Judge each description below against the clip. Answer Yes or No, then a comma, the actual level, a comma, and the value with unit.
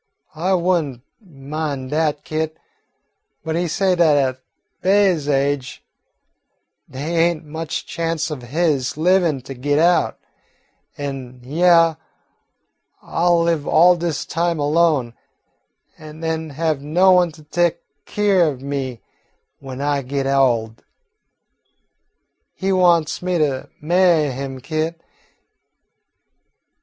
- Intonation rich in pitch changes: No, average, 3.6 semitones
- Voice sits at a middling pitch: Yes, medium, 155 Hz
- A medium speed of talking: No, slow, 120 wpm